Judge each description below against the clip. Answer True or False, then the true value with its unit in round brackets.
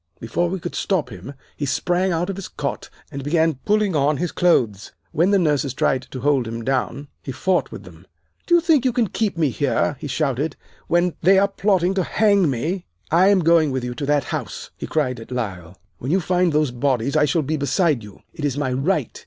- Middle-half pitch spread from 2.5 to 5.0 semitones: False (5.5 semitones)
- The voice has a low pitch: False (150 Hz)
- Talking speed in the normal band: False (225 wpm)